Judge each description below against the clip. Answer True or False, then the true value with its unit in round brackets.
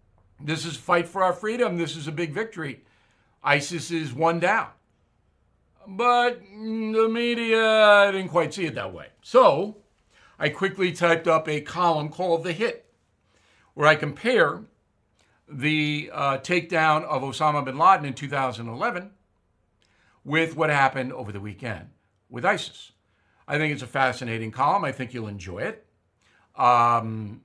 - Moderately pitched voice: True (155 Hz)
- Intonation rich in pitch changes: True (6.3 semitones)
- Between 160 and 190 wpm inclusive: False (145 wpm)